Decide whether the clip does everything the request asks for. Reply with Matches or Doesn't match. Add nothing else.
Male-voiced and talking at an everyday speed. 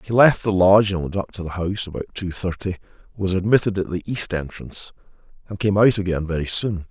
Doesn't match